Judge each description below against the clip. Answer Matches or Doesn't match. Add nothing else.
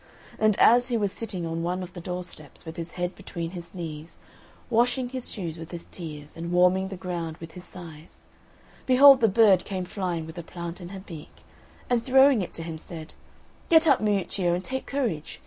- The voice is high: Doesn't match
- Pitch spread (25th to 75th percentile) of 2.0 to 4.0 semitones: Doesn't match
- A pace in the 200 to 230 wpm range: Matches